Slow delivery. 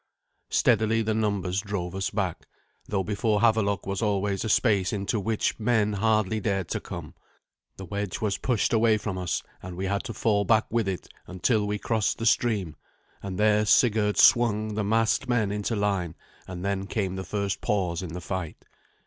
No: average, 185 wpm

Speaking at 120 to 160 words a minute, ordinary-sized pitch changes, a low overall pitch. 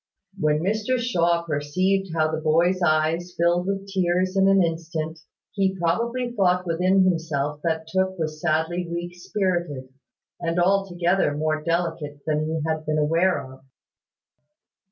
No: average, 140 wpm; average, 3.0 semitones; medium, 170 Hz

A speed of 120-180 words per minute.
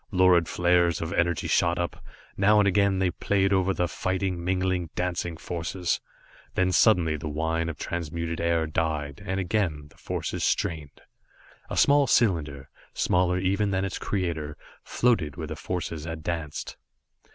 Yes: average, 150 wpm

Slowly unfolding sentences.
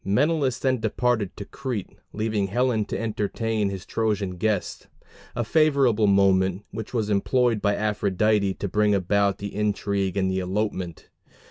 No: average, 145 wpm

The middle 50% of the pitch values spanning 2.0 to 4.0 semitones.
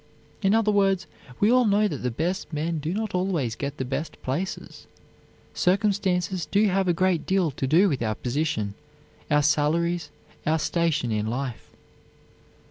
No: average, 5.3 semitones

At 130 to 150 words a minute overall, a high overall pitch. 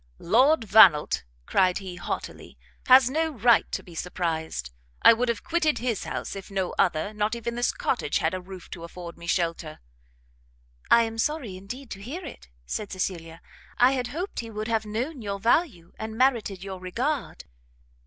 No: average, 175 wpm; high, 215 Hz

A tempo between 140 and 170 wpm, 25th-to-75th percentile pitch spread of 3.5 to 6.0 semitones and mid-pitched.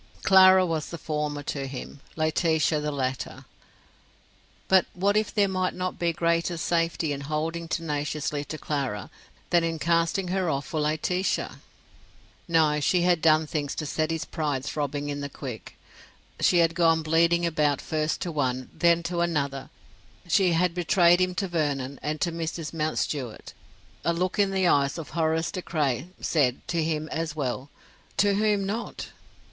No: average, 165 wpm; average, 2.8 semitones; medium, 160 Hz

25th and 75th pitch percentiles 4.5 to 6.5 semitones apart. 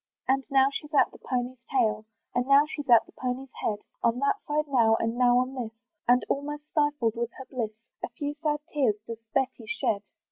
No: average, 3.2 semitones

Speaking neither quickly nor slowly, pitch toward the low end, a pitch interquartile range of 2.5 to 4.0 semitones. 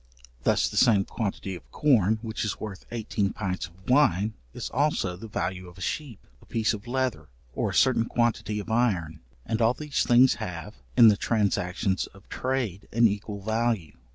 Yes: average, 180 wpm; low, 110 Hz; average, 3.6 semitones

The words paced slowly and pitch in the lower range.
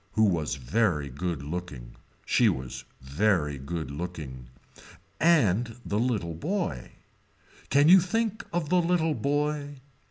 Yes: slow, 125 wpm; low, 100 Hz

